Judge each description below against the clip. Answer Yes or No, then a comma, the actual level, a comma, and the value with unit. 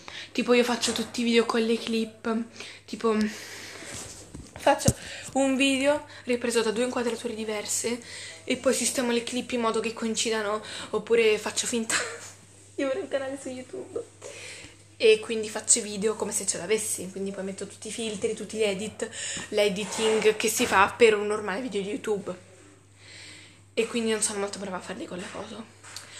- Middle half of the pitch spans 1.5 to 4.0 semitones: Yes, narrow, 2.6 semitones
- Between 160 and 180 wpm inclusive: Yes, fast, 170 wpm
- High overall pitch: Yes, high, 225 Hz